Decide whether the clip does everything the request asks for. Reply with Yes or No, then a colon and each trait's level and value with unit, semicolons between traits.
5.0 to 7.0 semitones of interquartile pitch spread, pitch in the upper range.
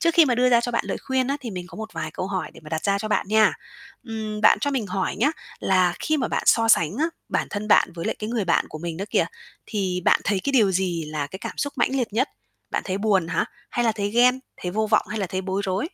No: average, 4.5 semitones; high, 210 Hz